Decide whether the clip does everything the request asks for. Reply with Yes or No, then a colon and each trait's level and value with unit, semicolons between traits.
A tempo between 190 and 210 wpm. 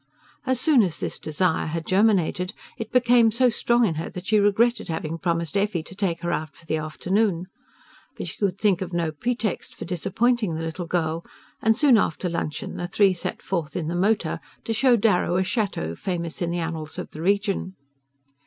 Yes: average, 200 wpm